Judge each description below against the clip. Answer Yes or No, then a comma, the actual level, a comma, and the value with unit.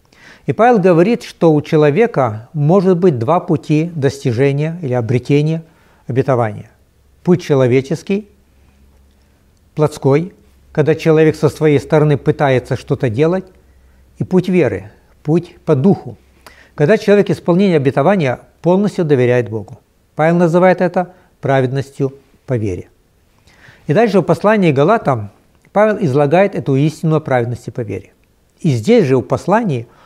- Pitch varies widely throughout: Yes, wide, 6.1 semitones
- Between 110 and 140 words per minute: Yes, average, 125 wpm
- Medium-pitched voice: Yes, medium, 145 Hz